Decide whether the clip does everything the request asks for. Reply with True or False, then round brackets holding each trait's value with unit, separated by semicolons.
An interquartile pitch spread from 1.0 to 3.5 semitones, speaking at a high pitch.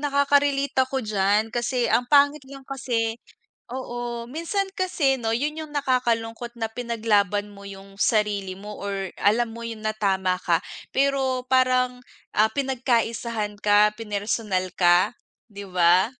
False (4.2 semitones; 230 Hz)